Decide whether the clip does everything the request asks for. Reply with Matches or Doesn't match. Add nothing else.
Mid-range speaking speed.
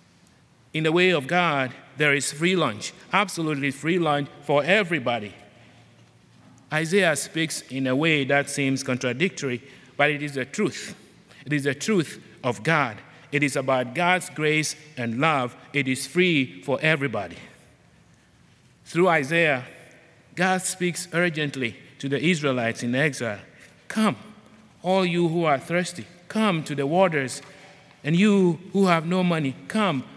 Matches